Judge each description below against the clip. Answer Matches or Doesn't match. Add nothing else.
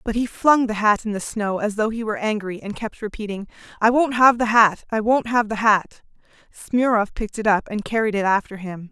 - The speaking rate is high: Matches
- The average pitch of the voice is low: Doesn't match